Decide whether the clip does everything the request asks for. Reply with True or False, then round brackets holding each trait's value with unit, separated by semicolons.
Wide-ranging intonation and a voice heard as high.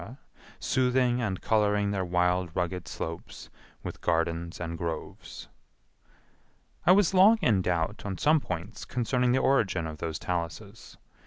False (6.3 semitones; 95 Hz)